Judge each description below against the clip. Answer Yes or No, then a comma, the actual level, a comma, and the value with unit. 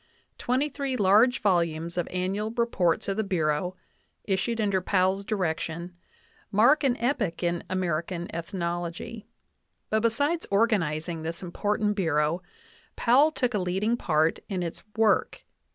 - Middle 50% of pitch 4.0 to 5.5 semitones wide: Yes, average, 4.6 semitones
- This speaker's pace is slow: Yes, slow, 130 wpm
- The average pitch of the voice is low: No, high, 190 Hz